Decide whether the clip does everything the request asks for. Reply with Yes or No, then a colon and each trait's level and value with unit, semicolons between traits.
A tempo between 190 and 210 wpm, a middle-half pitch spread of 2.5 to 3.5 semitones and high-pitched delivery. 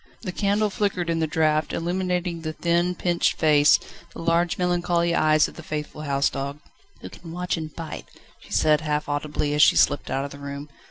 No: average, 200 wpm; average, 2.9 semitones; medium, 160 Hz